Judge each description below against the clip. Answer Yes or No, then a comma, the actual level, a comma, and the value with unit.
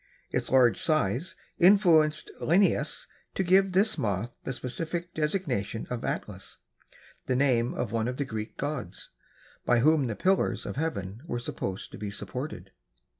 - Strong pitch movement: Yes, wide, 6.6 semitones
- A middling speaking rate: Yes, average, 150 wpm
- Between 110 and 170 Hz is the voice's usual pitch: Yes, low, 135 Hz